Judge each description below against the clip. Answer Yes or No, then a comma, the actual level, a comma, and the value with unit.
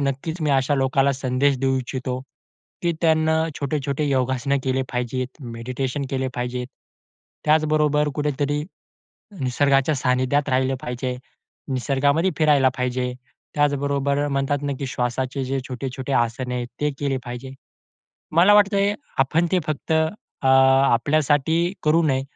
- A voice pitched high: No, low, 135 Hz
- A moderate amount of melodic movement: No, narrow, 2.3 semitones